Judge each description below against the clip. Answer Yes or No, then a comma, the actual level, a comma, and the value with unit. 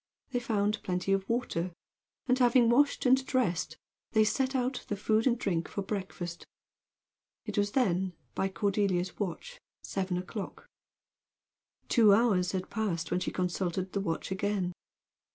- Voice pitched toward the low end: No, high, 200 Hz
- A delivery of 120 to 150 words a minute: Yes, average, 145 wpm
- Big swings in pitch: No, average, 4.3 semitones